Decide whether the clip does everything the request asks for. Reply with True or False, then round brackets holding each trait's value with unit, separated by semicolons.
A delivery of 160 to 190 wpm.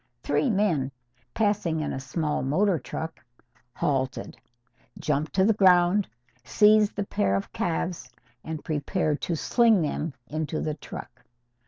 False (135 wpm)